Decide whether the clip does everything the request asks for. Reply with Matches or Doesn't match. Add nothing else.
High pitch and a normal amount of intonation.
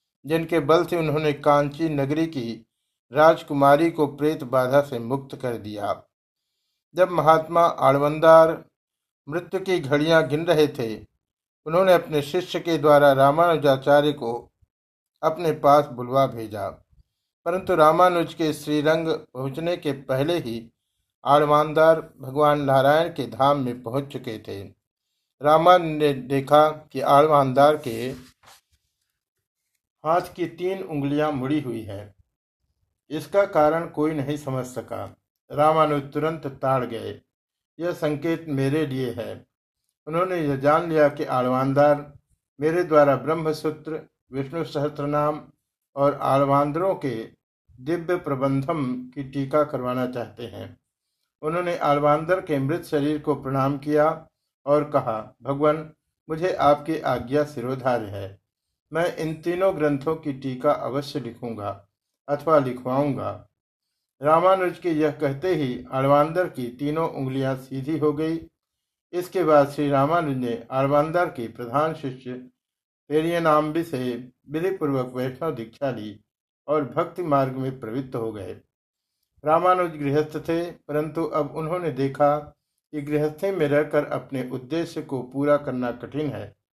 Doesn't match